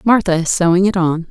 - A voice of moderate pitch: Yes, medium, 180 Hz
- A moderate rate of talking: No, fast, 230 wpm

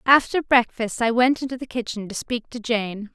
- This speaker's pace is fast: Yes, fast, 210 wpm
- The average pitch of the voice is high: Yes, high, 235 Hz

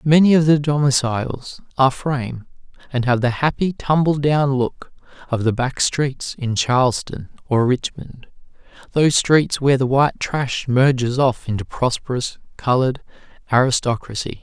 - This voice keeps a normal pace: No, slow, 130 wpm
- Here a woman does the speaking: No, male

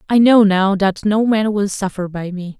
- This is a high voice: Yes, high, 200 Hz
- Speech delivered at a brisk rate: Yes, fast, 230 wpm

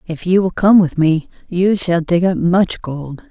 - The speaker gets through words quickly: Yes, fast, 220 wpm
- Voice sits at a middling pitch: Yes, medium, 175 Hz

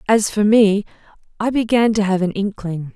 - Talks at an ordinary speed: Yes, average, 185 wpm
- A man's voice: No, female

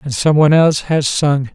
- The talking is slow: No, fast, 235 wpm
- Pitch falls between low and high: Yes, medium, 145 Hz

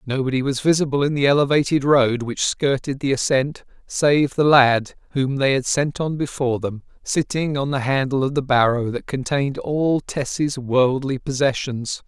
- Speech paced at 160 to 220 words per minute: Yes, average, 170 wpm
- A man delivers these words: Yes, male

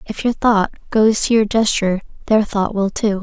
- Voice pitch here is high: Yes, high, 210 Hz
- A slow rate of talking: No, fast, 205 wpm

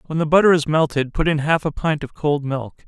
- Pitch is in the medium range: Yes, medium, 150 Hz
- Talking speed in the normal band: No, fast, 270 wpm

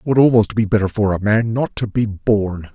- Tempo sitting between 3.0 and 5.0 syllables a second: No, 5.2 syllables/s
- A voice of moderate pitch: No, low, 105 Hz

